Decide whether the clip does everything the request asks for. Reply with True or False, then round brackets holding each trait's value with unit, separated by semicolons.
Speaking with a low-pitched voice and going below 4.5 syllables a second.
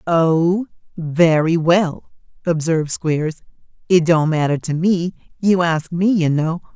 False (165 Hz; 4.0 syllables/s)